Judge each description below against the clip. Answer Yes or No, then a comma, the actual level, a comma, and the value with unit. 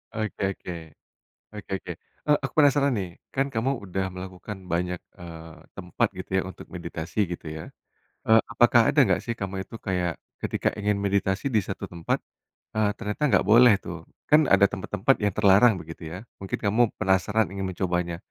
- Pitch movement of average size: Yes, average, 3.7 semitones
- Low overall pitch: Yes, low, 100 Hz